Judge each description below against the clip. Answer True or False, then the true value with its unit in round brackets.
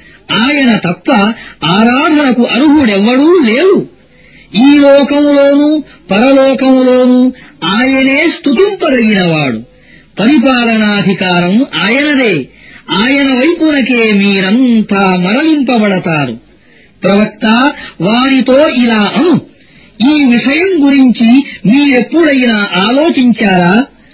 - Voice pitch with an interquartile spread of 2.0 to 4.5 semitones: False (5.3 semitones)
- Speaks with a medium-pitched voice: False (250 Hz)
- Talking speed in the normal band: False (60 wpm)